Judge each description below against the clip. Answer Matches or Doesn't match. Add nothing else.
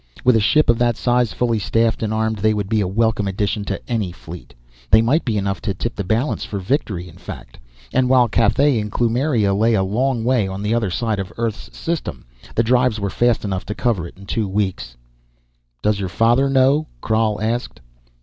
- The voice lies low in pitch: Matches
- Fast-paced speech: Matches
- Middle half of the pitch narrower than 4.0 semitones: Matches